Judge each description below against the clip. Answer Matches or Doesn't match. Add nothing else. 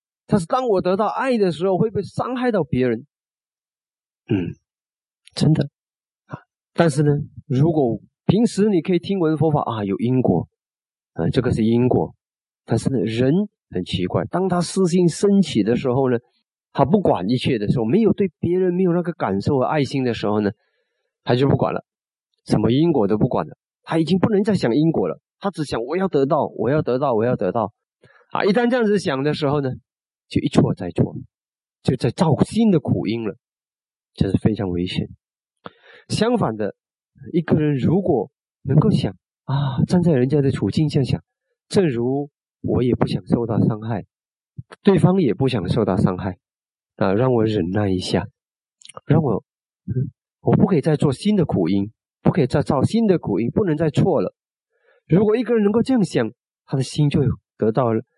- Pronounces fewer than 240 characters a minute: Doesn't match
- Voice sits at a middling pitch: Matches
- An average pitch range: Doesn't match